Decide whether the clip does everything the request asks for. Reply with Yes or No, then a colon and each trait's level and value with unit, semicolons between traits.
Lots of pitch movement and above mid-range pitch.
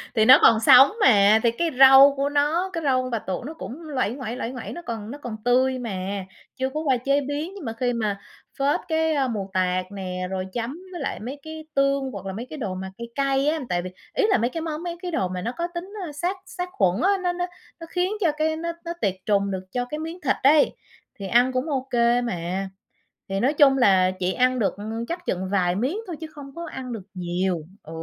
Yes: wide, 7.2 semitones; very high, 255 Hz